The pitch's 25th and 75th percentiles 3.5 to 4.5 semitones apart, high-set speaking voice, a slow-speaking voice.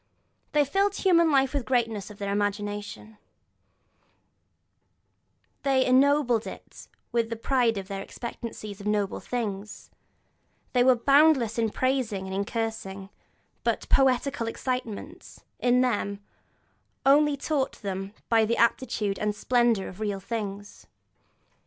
Yes: average, 4.2 semitones; high, 230 Hz; slow, 125 wpm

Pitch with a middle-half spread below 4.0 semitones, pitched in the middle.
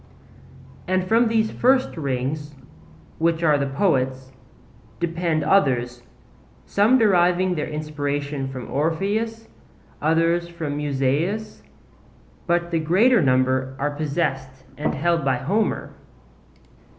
No: average, 5.0 semitones; medium, 155 Hz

